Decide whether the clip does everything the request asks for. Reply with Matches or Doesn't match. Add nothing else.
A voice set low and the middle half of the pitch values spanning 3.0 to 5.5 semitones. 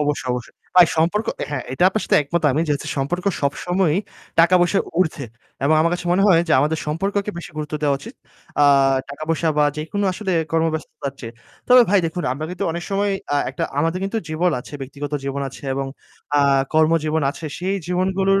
Doesn't match